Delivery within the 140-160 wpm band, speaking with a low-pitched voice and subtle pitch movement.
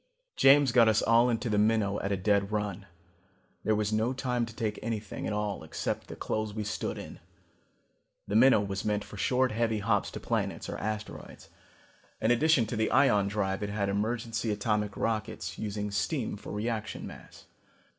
No: average, 180 wpm; low, 105 Hz; narrow, 1.9 semitones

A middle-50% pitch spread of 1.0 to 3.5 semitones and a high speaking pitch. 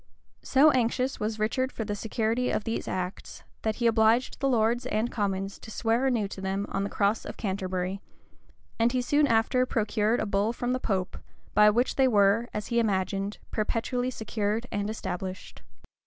Yes: average, 3.1 semitones; high, 220 Hz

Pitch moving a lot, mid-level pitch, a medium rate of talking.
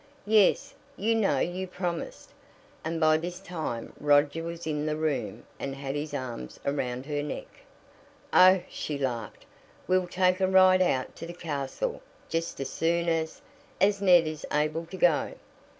No: average, 4.0 semitones; medium, 165 Hz; average, 160 wpm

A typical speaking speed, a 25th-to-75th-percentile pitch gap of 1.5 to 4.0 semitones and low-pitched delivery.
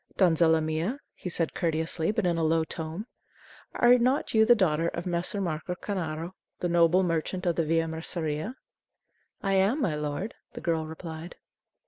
No: average, 165 wpm; average, 2.9 semitones; medium, 170 Hz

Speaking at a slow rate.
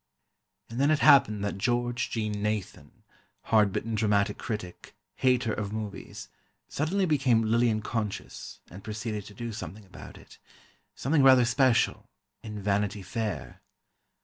Yes: slow, 125 wpm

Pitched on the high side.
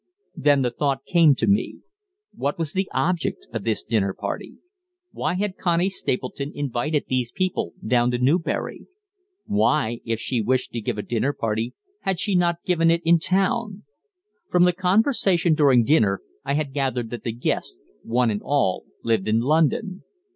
No: medium, 145 Hz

